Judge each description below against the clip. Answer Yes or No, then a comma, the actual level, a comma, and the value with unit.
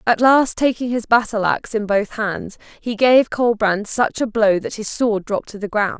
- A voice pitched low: No, high, 220 Hz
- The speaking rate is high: Yes, fast, 220 wpm